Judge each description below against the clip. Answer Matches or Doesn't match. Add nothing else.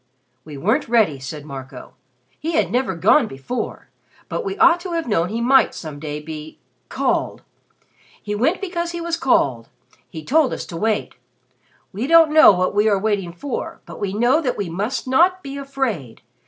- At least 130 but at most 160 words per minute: Doesn't match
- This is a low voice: Doesn't match